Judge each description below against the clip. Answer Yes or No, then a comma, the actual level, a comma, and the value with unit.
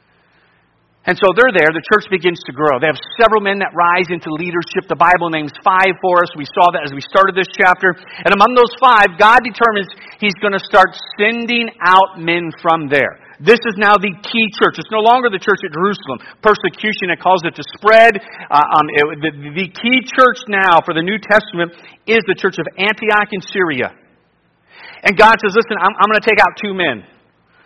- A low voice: No, high, 190 Hz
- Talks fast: Yes, fast, 210 wpm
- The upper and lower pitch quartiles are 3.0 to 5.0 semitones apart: Yes, average, 3.9 semitones